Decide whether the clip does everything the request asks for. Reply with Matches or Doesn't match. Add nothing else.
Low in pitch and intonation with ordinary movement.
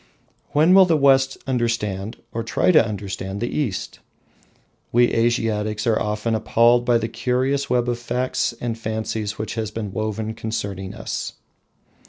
Doesn't match